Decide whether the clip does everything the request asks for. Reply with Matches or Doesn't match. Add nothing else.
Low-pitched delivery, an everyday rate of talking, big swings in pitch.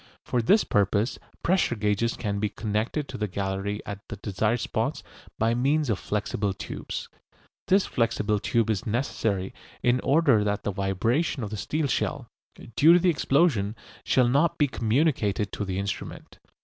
Doesn't match